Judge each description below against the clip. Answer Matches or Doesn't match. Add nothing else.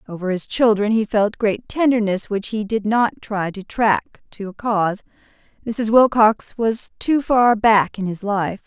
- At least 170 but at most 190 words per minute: Matches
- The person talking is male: Doesn't match